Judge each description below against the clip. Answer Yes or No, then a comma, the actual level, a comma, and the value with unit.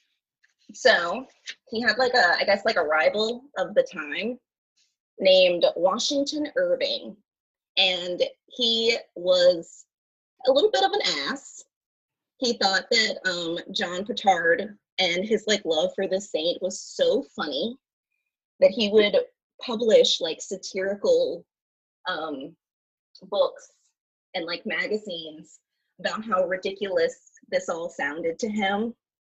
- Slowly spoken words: Yes, slow, 125 wpm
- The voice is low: No, high, 225 Hz